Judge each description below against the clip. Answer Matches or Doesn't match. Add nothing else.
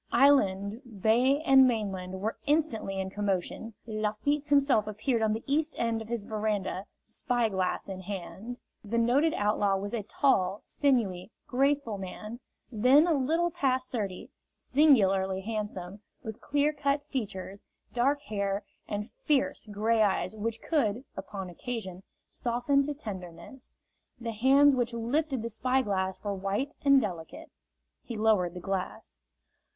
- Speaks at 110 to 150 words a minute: Matches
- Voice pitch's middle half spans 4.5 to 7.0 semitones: Matches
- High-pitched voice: Matches